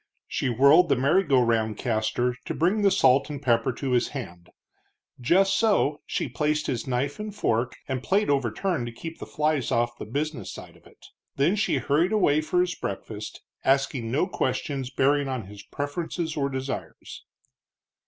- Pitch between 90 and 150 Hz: Yes, medium, 140 Hz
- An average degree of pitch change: Yes, average, 4.5 semitones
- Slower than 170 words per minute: No, average, 175 wpm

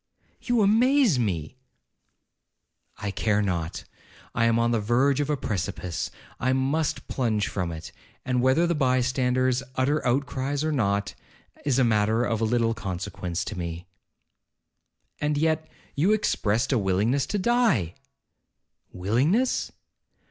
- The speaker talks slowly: Yes, slow, 125 wpm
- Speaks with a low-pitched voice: Yes, low, 125 Hz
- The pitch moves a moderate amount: No, wide, 5.8 semitones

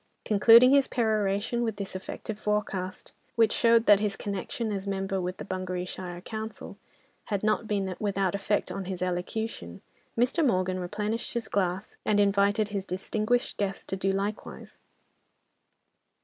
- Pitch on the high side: Yes, high, 200 Hz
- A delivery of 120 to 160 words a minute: Yes, average, 145 wpm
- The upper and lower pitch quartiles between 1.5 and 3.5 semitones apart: Yes, narrow, 2.5 semitones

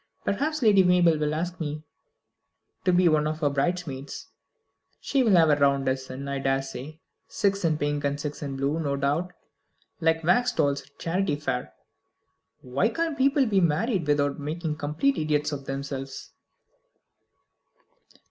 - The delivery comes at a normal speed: Yes, average, 150 wpm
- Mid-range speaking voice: Yes, medium, 150 Hz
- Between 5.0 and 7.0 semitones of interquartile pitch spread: No, average, 4.2 semitones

